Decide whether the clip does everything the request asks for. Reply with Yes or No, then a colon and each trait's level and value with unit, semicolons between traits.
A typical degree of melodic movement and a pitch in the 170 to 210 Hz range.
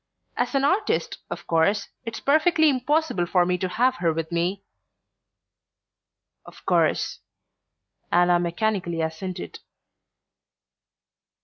No: wide, 7.8 semitones; medium, 185 Hz